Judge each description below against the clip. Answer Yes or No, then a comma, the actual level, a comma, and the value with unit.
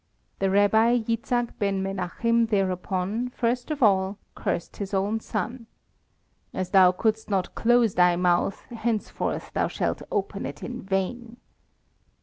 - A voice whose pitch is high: Yes, high, 210 Hz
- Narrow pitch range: No, average, 3.5 semitones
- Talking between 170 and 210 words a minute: No, slow, 135 wpm